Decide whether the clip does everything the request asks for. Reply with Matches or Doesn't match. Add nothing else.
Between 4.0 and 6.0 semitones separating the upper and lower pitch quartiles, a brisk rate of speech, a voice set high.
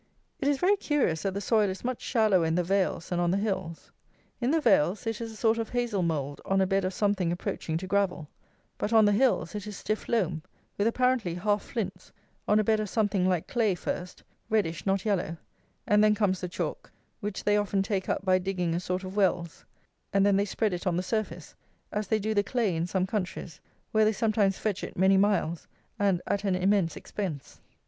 Doesn't match